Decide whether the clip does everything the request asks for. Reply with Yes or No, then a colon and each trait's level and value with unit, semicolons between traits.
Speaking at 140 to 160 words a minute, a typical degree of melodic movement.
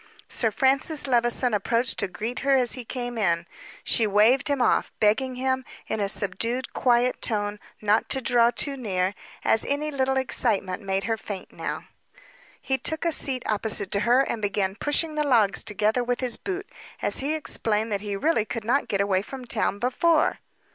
No: average, 185 wpm; average, 4.2 semitones